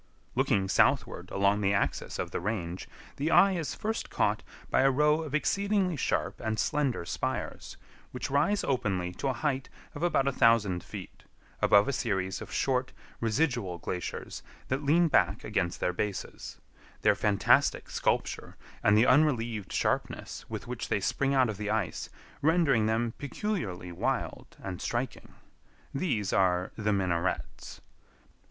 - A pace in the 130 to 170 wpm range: Yes, average, 150 wpm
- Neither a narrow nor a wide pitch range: No, wide, 6.5 semitones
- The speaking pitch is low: Yes, low, 115 Hz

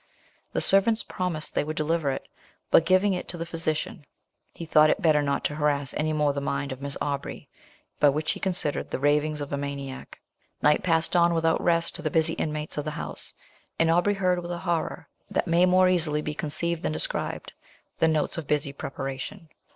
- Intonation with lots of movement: No, average, 2.7 semitones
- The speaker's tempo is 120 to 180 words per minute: No, fast, 205 wpm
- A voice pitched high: No, medium, 155 Hz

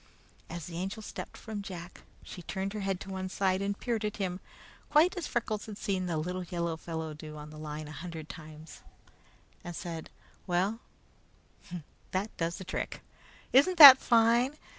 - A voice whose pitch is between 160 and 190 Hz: Yes, medium, 185 Hz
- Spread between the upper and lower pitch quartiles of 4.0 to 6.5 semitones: Yes, average, 4.3 semitones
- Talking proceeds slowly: No, average, 175 wpm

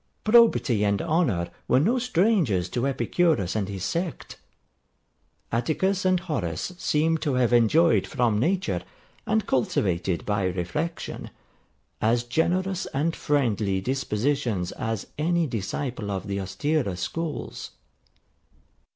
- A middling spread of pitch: No, wide, 8.6 semitones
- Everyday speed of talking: No, slow, 115 wpm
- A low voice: Yes, low, 130 Hz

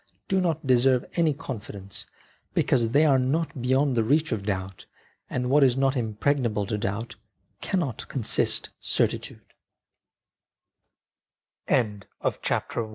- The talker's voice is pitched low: Yes, low, 130 Hz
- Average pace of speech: No, slow, 105 wpm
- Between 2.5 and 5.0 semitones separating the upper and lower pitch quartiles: Yes, average, 4.5 semitones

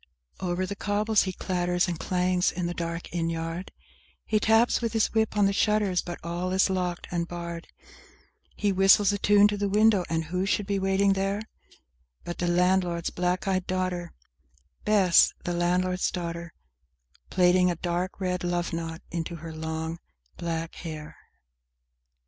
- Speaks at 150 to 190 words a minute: Yes, average, 165 wpm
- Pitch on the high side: No, medium, 180 Hz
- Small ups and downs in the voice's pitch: Yes, narrow, 2.3 semitones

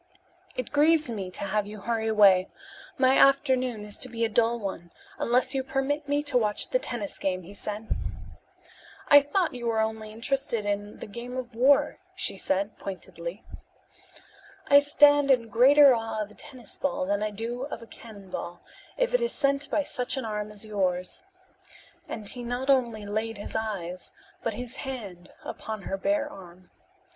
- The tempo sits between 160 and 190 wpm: Yes, average, 175 wpm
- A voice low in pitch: No, high, 230 Hz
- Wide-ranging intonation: No, average, 4.6 semitones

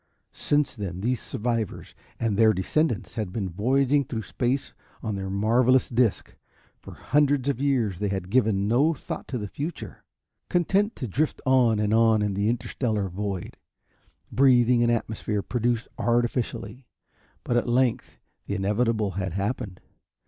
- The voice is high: No, low, 115 Hz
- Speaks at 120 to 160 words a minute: Yes, average, 150 wpm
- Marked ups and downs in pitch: No, average, 3.8 semitones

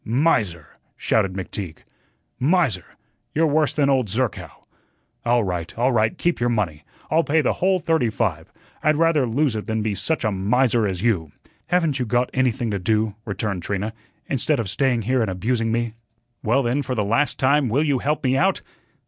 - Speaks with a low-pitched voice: Yes, low, 120 Hz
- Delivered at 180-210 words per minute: Yes, average, 185 wpm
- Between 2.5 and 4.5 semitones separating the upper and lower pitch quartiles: No, average, 5.1 semitones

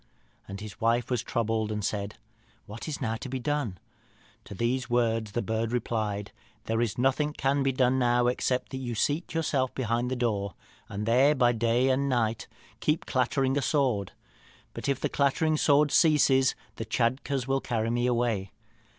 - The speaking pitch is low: Yes, low, 120 Hz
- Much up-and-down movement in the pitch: No, average, 3.0 semitones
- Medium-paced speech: Yes, average, 175 wpm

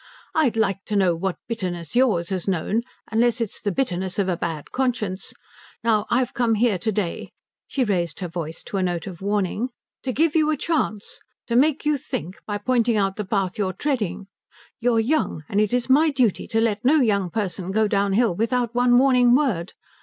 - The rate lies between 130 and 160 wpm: No, fast, 205 wpm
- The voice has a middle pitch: No, high, 215 Hz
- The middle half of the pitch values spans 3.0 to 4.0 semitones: No, average, 4.6 semitones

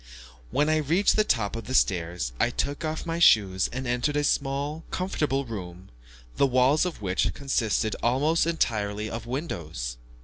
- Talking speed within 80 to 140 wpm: No, average, 165 wpm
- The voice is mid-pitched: No, low, 130 Hz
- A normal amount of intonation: No, wide, 6.6 semitones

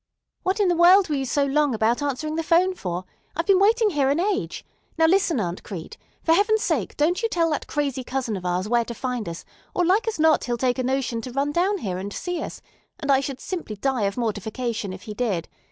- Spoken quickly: Yes, fast, 240 wpm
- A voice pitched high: Yes, very high, 275 Hz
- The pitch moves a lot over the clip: Yes, wide, 7.2 semitones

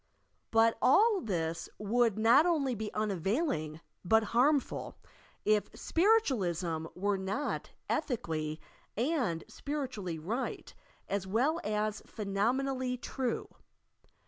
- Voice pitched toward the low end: No, high, 220 Hz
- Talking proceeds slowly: Yes, slow, 100 wpm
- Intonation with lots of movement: Yes, wide, 5.9 semitones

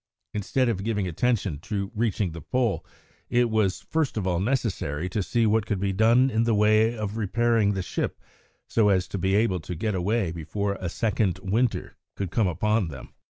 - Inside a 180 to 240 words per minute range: Yes, average, 195 wpm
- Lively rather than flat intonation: No, average, 3.4 semitones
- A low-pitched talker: Yes, low, 105 Hz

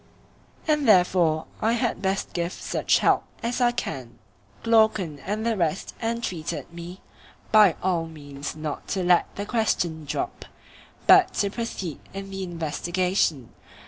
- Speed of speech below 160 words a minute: Yes, average, 140 wpm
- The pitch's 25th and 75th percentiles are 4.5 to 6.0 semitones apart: Yes, average, 5.2 semitones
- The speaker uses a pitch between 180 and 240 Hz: Yes, medium, 185 Hz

